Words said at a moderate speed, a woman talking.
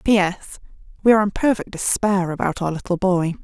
Yes: average, 175 wpm; female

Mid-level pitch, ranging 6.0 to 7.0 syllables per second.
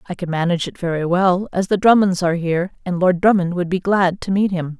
Yes: medium, 180 Hz; 6.1 syllables/s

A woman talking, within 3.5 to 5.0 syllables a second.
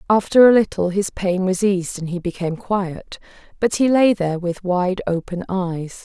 Yes: female; 4.9 syllables/s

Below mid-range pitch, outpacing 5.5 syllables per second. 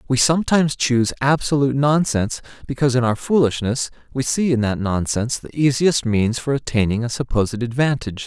Yes: low, 130 Hz; 6.0 syllables/s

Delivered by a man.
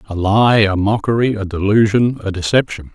Yes: male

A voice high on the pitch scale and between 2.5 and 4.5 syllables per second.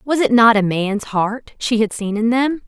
Yes: high, 230 Hz; 4.3 syllables/s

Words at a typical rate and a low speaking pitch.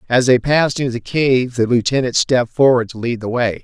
No: fast, 230 wpm; low, 125 Hz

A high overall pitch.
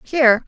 Yes: very high, 255 Hz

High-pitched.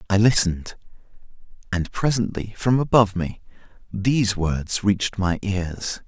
No: low, 100 Hz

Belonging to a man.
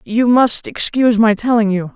No: female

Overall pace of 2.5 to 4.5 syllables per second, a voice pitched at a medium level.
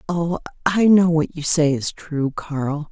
Yes: 3.7 syllables/s; medium, 160 Hz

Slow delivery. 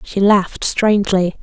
Yes: slow, 125 wpm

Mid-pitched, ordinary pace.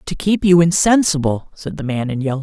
No: medium, 160 Hz; fast, 225 wpm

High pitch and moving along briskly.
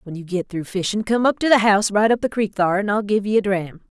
Yes: high, 205 Hz; fast, 320 wpm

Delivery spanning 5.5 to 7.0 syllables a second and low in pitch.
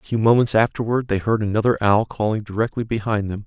Yes: 6.3 syllables/s; low, 110 Hz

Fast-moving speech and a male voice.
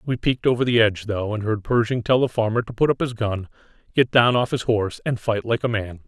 Yes: fast, 265 wpm; male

